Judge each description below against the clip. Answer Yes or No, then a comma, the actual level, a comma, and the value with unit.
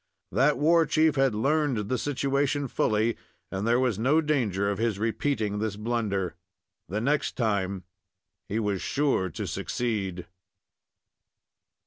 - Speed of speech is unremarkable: No, slow, 130 wpm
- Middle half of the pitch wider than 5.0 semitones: Yes, wide, 5.4 semitones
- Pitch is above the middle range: No, low, 115 Hz